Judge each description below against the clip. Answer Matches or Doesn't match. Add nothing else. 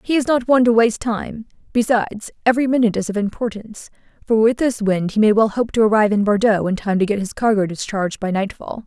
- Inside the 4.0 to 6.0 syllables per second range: Doesn't match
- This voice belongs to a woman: Matches